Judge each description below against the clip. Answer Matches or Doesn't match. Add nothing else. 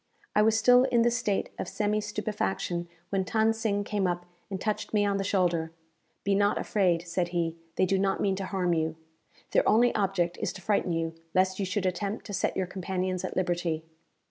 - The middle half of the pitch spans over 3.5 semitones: Doesn't match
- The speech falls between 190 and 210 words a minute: Matches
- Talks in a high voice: Matches